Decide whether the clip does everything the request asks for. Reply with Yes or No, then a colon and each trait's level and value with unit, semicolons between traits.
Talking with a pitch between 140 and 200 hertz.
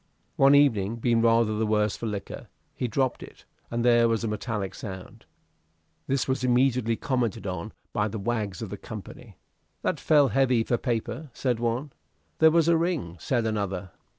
No: low, 115 Hz